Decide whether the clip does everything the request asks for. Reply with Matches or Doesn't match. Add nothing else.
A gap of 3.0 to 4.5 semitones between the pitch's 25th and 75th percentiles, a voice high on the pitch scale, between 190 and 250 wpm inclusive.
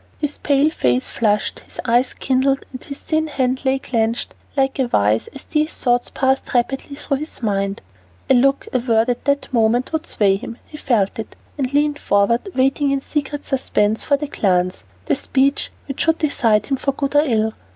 Matches